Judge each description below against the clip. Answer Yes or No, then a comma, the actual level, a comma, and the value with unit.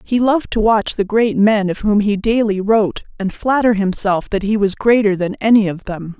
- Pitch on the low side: No, high, 210 Hz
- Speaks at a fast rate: Yes, fast, 225 wpm